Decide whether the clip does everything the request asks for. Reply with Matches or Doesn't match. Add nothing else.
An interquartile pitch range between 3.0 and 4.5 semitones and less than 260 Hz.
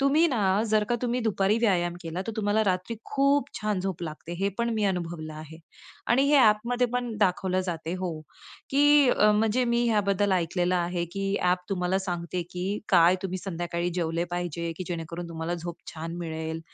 Matches